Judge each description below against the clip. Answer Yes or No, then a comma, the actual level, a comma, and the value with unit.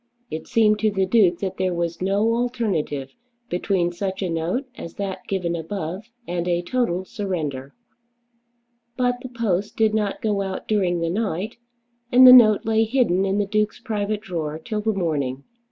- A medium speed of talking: Yes, average, 170 wpm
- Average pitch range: Yes, average, 4.1 semitones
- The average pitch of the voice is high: Yes, high, 195 Hz